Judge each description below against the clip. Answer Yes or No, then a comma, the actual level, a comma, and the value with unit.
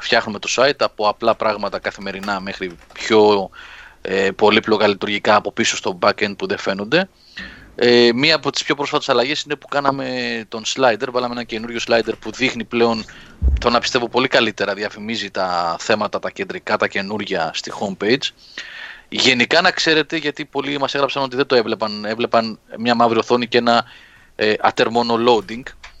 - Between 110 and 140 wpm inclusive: No, average, 165 wpm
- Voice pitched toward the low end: Yes, low, 115 Hz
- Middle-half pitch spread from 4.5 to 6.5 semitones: No, average, 4.1 semitones